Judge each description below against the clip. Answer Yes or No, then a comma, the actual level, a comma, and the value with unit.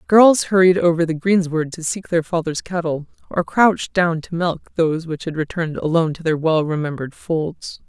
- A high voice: No, medium, 165 Hz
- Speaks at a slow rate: No, average, 190 wpm